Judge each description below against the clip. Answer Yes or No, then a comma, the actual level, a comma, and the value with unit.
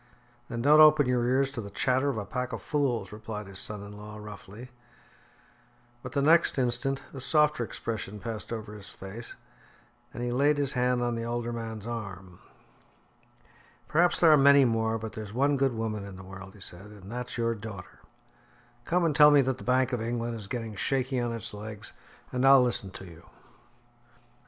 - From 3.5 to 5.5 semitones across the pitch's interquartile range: Yes, average, 3.9 semitones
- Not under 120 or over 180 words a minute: No, average, 195 wpm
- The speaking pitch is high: No, low, 120 Hz